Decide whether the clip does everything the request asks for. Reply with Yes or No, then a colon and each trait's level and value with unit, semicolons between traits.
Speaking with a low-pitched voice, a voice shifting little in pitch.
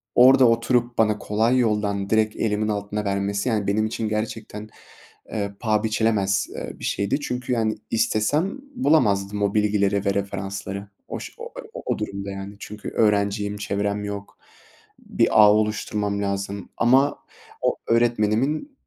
Yes: low, 105 Hz; narrow, 2.0 semitones